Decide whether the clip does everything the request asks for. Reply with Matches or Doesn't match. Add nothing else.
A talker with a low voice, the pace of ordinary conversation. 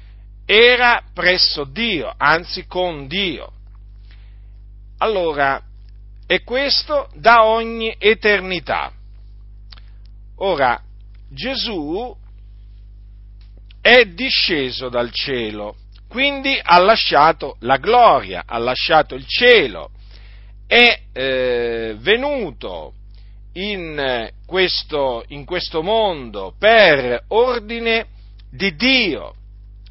Doesn't match